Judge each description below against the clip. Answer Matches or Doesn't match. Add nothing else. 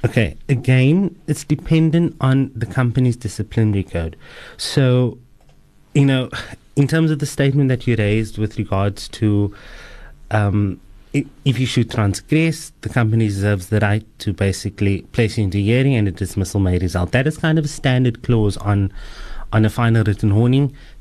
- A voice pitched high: Doesn't match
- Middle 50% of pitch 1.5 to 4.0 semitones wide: Doesn't match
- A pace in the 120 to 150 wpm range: Doesn't match